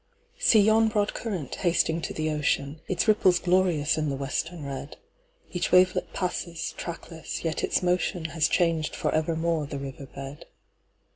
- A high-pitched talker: No, medium, 165 Hz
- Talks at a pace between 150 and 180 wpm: No, average, 140 wpm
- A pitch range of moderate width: Yes, average, 3.2 semitones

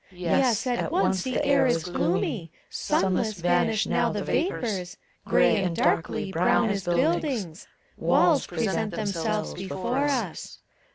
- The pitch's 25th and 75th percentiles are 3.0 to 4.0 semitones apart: No, average, 5.2 semitones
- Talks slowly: Yes, slow, 125 wpm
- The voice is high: Yes, high, 200 Hz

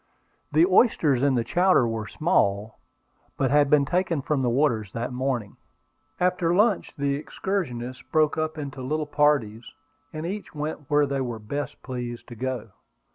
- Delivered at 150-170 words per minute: Yes, average, 165 wpm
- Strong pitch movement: No, average, 4.3 semitones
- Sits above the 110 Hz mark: Yes, medium, 140 Hz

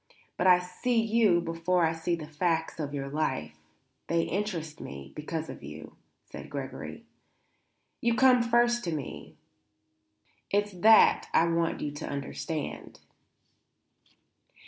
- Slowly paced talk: Yes, slow, 130 wpm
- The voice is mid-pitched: Yes, medium, 170 Hz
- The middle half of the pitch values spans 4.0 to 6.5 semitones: Yes, average, 5.2 semitones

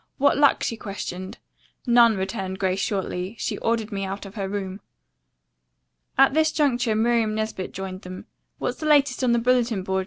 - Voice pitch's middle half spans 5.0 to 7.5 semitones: No, average, 4.0 semitones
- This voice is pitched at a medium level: No, high, 215 Hz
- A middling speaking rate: Yes, average, 175 wpm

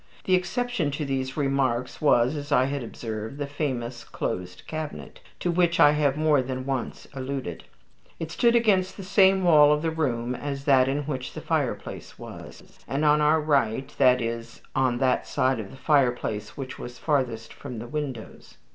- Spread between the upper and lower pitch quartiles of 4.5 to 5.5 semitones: No, average, 3.6 semitones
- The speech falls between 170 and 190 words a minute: Yes, average, 180 wpm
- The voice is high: No, medium, 140 Hz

